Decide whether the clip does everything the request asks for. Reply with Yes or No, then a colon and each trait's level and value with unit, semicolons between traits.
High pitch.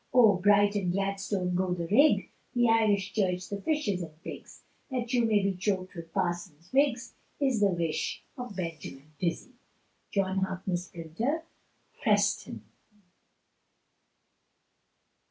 Yes: high, 195 Hz